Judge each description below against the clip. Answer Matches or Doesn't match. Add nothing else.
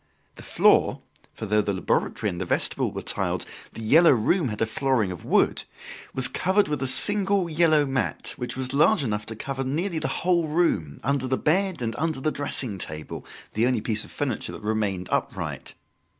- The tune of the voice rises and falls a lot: Matches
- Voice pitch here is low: Matches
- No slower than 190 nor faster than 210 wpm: Matches